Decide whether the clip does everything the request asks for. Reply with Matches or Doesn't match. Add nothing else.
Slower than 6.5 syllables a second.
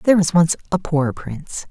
Matches